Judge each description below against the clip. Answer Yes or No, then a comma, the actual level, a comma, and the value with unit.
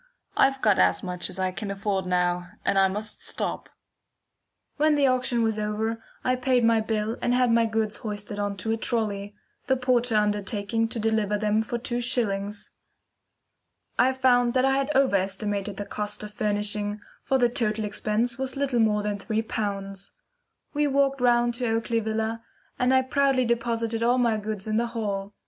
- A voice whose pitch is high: Yes, high, 220 Hz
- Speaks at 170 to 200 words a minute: Yes, average, 180 wpm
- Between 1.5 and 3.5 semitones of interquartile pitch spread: Yes, average, 3.0 semitones